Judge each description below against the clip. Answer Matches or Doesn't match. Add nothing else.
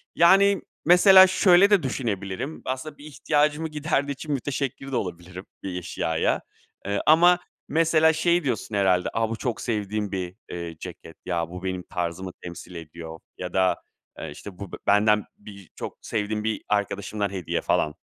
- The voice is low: Matches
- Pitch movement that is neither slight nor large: Doesn't match